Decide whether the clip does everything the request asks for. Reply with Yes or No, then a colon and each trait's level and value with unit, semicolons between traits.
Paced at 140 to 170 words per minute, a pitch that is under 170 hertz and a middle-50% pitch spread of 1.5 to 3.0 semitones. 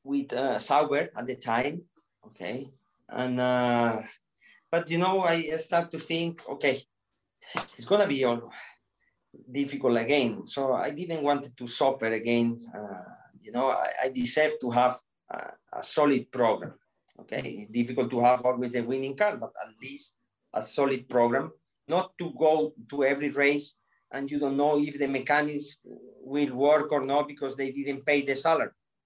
No: average, 165 wpm; medium, 140 Hz; average, 3.4 semitones